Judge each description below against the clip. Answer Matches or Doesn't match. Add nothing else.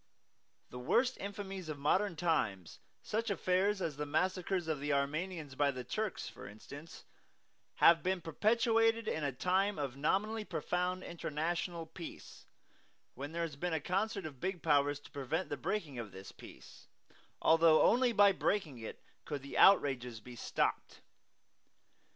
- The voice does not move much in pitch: Doesn't match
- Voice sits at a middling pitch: Matches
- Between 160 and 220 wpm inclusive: Doesn't match